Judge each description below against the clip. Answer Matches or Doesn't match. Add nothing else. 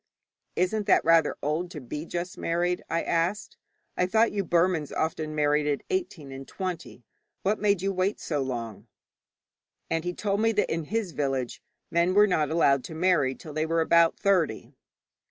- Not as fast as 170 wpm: Doesn't match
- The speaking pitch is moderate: Matches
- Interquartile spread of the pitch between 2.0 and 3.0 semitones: Doesn't match